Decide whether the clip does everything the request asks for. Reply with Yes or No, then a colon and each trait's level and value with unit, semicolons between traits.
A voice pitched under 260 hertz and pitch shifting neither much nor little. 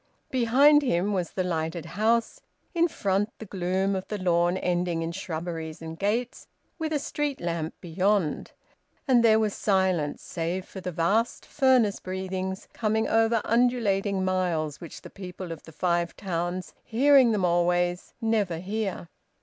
Yes: high, 190 Hz; average, 4.3 semitones